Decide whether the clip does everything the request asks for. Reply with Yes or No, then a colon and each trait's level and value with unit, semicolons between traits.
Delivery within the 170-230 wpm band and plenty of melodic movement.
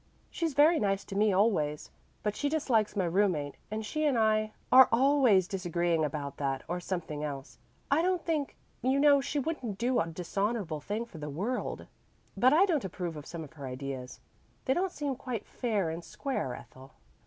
Yes: average, 190 wpm; wide, 8.4 semitones